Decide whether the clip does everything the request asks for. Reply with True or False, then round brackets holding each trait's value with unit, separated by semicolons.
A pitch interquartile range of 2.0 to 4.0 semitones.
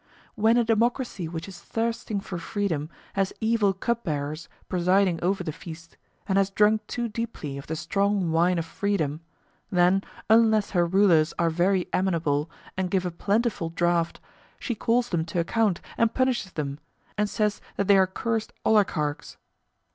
False (4.4 semitones)